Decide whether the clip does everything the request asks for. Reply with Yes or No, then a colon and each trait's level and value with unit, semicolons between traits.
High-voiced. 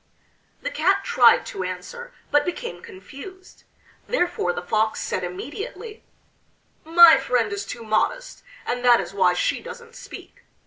Yes: very high, 255 Hz